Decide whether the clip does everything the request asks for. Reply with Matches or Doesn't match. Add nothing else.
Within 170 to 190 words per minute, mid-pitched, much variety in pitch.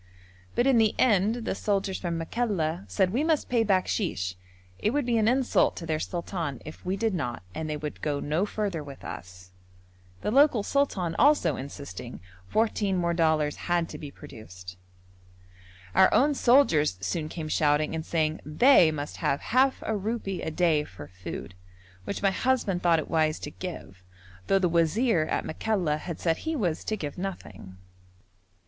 Matches